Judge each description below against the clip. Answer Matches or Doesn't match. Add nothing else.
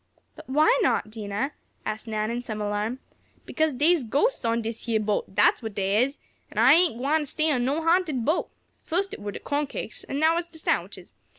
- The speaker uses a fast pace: Matches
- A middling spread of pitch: Doesn't match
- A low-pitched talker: Doesn't match